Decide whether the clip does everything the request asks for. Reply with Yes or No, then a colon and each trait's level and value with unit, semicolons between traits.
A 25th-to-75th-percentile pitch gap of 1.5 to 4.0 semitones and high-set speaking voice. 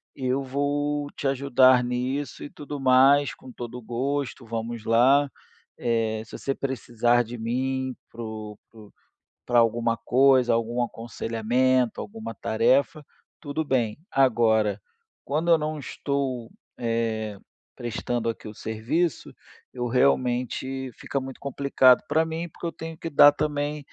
No: average, 3.3 semitones; low, 130 Hz